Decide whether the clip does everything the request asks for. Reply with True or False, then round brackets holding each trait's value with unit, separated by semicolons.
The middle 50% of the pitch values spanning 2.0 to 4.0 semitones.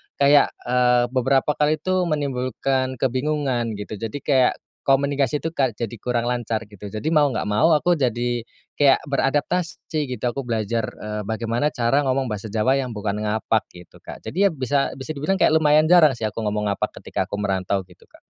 False (4.7 semitones)